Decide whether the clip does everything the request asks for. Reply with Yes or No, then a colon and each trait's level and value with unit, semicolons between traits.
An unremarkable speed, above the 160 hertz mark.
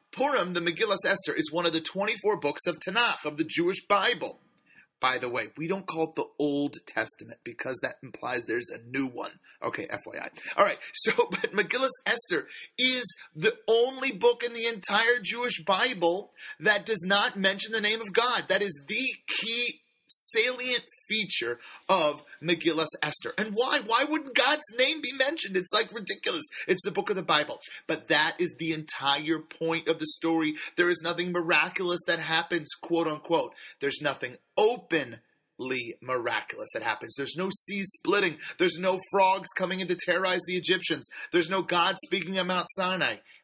Yes: average, 175 wpm; high, 190 Hz